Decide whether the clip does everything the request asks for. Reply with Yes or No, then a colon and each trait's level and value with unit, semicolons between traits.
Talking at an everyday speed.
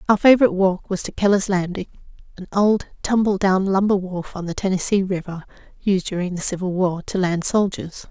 Yes: average, 180 wpm